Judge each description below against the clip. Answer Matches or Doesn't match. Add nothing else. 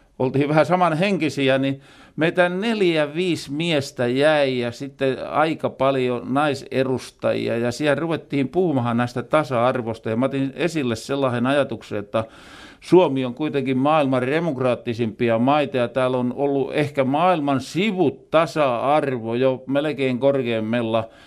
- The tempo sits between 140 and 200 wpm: Doesn't match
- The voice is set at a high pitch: Doesn't match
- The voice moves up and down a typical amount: Matches